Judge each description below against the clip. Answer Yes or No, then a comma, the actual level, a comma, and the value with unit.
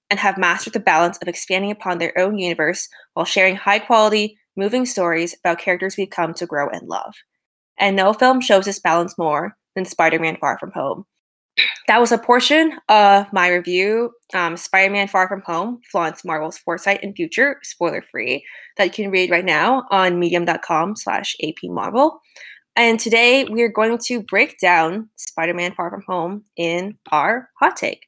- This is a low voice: No, high, 190 Hz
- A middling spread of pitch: Yes, average, 4.0 semitones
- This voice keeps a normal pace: Yes, average, 165 wpm